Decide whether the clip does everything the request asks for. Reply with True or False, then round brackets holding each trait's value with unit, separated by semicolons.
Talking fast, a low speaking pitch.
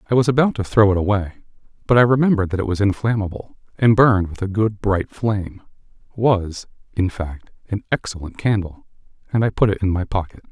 False (185 wpm; 100 Hz)